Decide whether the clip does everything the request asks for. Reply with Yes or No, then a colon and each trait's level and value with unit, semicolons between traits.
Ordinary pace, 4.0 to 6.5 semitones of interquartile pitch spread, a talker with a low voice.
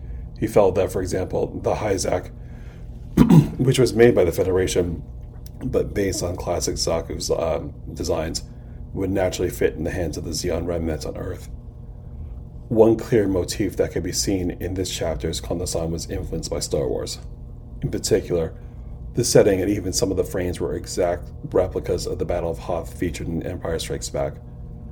Yes: average, 175 wpm; average, 4.9 semitones; very low, 85 Hz